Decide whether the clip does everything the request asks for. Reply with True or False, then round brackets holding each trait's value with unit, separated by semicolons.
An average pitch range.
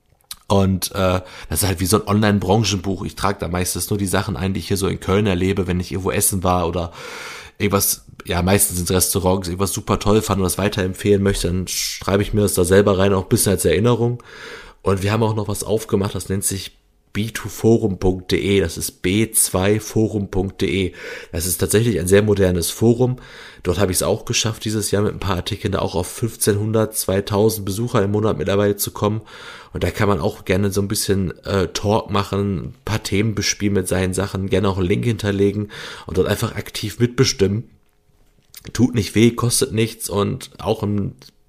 False (2.3 semitones)